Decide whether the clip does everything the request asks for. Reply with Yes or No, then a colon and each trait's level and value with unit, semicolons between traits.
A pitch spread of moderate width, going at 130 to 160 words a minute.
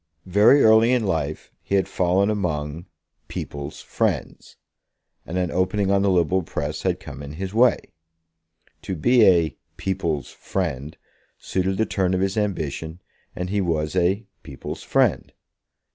Yes: average, 3.7 semitones; average, 145 wpm